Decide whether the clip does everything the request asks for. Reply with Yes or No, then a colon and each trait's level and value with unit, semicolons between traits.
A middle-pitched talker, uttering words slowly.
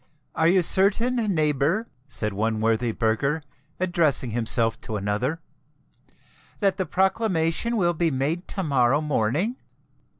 Yes: medium, 155 Hz; slow, 125 wpm